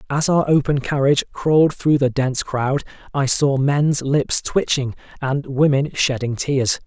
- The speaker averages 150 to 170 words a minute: Yes, average, 155 wpm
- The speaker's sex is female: No, male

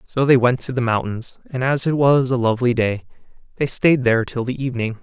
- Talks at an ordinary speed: No, fast, 225 wpm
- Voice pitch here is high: No, low, 125 Hz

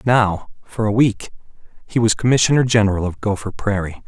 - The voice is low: Yes, low, 110 Hz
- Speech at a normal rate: Yes, average, 160 wpm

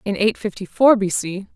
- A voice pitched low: No, high, 200 Hz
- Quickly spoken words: Yes, fast, 230 wpm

